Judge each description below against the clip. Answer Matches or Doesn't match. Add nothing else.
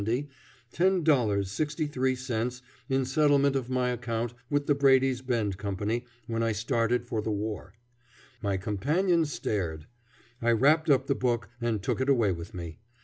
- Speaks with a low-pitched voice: Matches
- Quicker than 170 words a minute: Doesn't match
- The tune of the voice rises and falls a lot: Doesn't match